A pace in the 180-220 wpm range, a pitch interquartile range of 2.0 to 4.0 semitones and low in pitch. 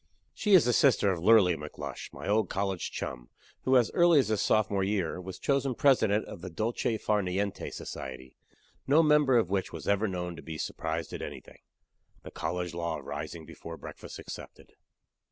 No: average, 185 wpm; average, 5.3 semitones; low, 100 Hz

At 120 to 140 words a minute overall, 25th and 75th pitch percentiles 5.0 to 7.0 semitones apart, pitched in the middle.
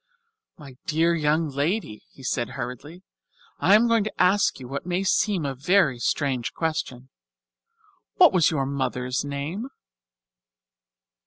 Yes: slow, 135 wpm; wide, 5.5 semitones; medium, 150 Hz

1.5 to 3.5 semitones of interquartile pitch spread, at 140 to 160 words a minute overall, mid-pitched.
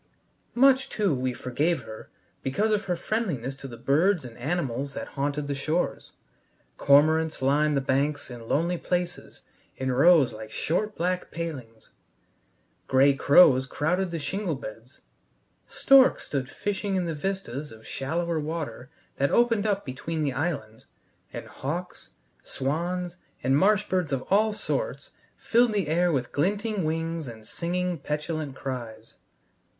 No: average, 5.2 semitones; average, 145 wpm; medium, 155 Hz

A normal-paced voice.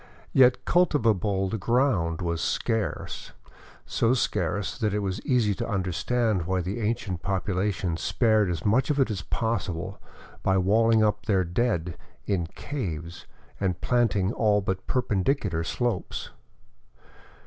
No: slow, 125 wpm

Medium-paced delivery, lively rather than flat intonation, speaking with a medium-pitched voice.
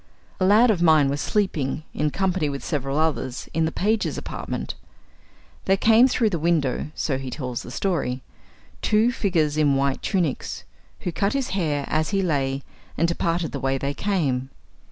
Yes: average, 175 wpm; wide, 5.7 semitones; medium, 160 Hz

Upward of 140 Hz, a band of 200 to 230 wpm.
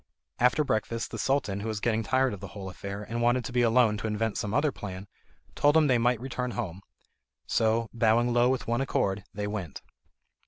No: low, 115 Hz; fast, 205 wpm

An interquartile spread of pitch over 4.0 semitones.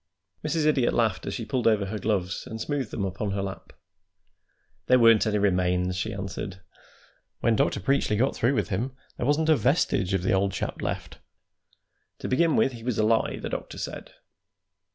Yes: average, 4.8 semitones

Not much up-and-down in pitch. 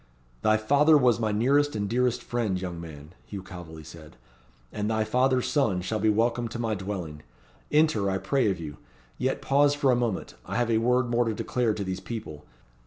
No: average, 4.8 semitones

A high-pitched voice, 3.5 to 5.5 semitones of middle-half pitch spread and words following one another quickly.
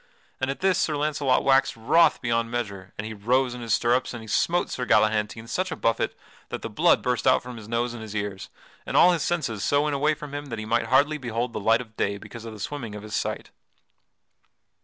No: low, 120 Hz; average, 4.3 semitones; fast, 235 wpm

